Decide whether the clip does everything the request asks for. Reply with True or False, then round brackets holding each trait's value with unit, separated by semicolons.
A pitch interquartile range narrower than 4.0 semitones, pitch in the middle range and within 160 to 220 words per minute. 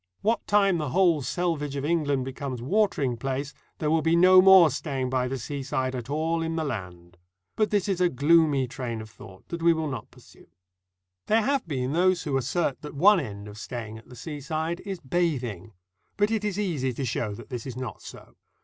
False (5.3 semitones; 145 Hz; 205 wpm)